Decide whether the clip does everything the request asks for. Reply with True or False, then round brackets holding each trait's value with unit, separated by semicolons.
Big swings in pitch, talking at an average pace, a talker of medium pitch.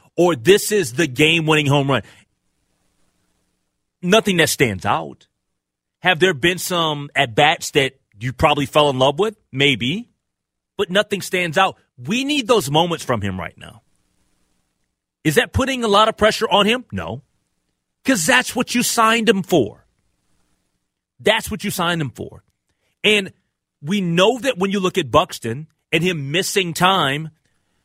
True (7.3 semitones; 160 wpm; 165 Hz)